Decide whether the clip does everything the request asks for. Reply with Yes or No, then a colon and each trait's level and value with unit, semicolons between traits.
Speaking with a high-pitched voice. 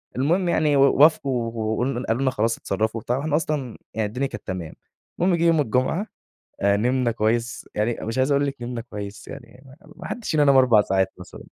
No: low, 125 Hz